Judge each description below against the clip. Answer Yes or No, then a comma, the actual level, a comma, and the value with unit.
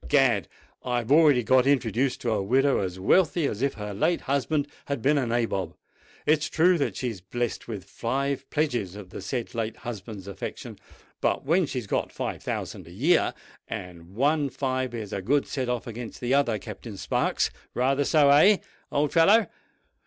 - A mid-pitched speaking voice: No, low, 125 Hz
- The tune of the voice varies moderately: Yes, average, 4.9 semitones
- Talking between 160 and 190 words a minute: Yes, average, 170 wpm